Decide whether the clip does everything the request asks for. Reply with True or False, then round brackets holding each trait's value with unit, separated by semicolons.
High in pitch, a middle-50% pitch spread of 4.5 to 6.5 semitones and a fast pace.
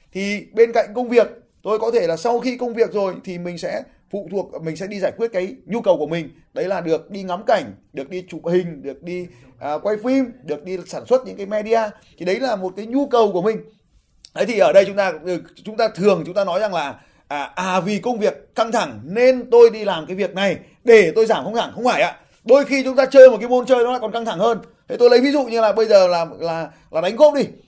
True (205 Hz; 4.9 semitones; 275 wpm)